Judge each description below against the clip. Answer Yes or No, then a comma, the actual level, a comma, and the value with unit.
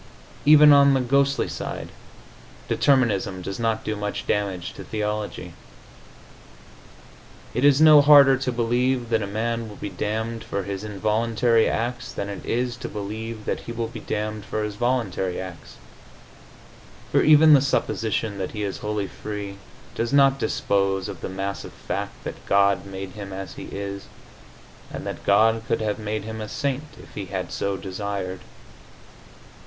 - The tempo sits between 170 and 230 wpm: No, average, 160 wpm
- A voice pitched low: Yes, low, 110 Hz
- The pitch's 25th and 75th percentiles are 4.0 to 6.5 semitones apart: No, average, 3.4 semitones